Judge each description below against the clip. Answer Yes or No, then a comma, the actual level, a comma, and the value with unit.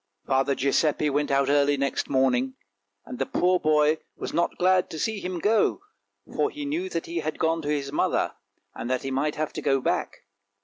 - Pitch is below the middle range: No, medium, 150 Hz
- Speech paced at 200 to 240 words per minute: Yes, fast, 205 wpm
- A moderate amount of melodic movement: Yes, average, 4.6 semitones